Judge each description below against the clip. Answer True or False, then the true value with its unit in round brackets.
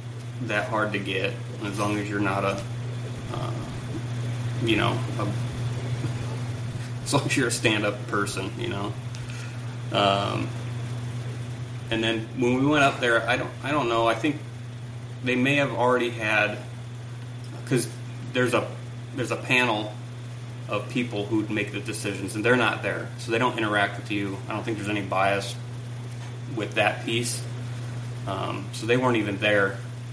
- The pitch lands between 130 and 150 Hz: False (120 Hz)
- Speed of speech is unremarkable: True (160 wpm)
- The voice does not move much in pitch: True (1.2 semitones)